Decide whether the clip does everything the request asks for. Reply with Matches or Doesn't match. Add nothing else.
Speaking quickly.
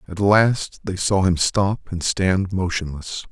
Doesn't match